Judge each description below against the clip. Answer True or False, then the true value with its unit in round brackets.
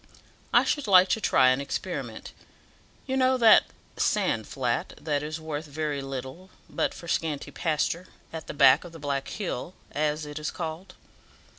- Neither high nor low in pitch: True (155 Hz)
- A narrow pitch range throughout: False (4.1 semitones)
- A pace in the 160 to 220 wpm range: True (165 wpm)